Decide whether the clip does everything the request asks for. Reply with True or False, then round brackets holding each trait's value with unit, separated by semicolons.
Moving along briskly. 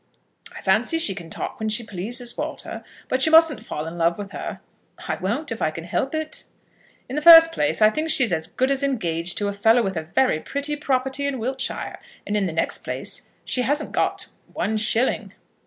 True (215 wpm)